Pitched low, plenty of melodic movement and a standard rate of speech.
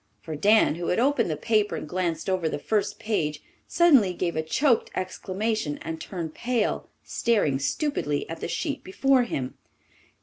No: medium, 185 Hz; wide, 6.1 semitones; average, 165 wpm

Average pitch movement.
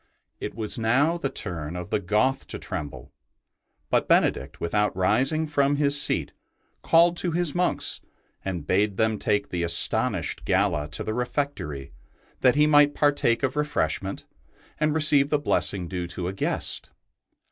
No: wide, 8.1 semitones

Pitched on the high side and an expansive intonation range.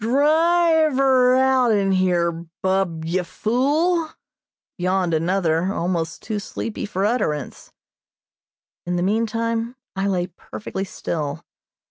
Yes: high, 200 Hz; wide, 6.1 semitones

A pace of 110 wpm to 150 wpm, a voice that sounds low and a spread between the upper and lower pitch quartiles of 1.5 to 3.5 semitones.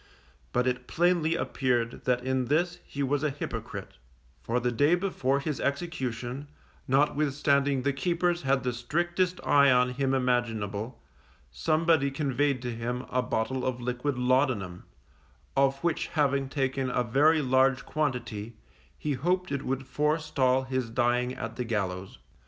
Yes: average, 145 wpm; low, 130 Hz; average, 2.9 semitones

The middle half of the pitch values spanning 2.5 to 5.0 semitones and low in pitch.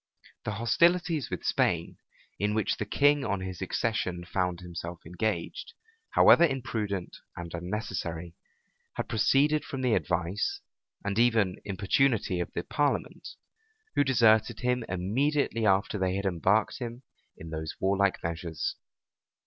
No: wide, 5.5 semitones; low, 105 Hz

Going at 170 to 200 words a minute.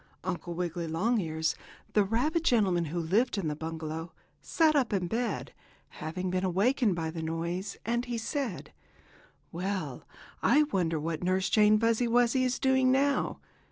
No: average, 155 wpm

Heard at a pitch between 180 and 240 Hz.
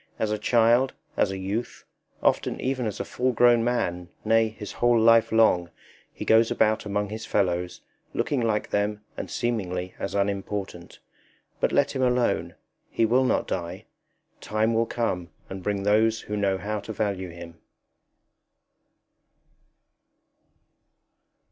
No: low, 105 Hz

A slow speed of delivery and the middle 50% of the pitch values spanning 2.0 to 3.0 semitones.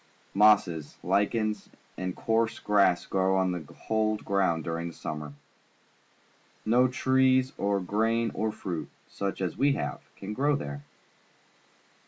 No: slow, 130 wpm; average, 4.1 semitones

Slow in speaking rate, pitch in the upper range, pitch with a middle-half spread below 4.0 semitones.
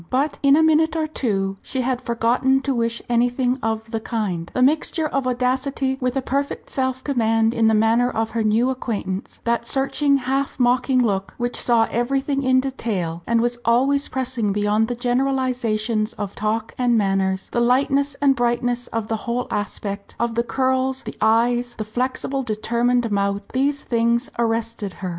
No: average, 175 wpm; high, 240 Hz; average, 2.8 semitones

